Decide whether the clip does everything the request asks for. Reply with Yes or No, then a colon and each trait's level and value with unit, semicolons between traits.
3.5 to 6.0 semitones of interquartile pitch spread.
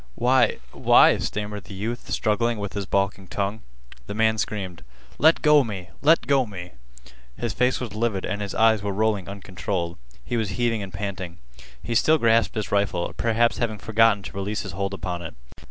No: average, 2.9 semitones